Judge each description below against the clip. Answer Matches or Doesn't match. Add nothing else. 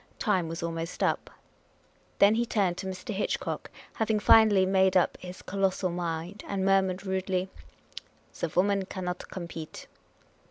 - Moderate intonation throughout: Doesn't match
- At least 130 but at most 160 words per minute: Matches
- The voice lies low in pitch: Doesn't match